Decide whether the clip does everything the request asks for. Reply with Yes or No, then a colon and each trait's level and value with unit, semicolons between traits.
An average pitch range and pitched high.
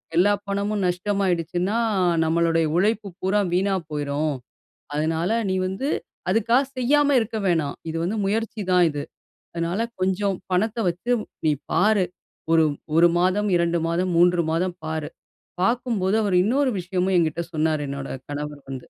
No: average, 3.9 semitones; medium, 180 Hz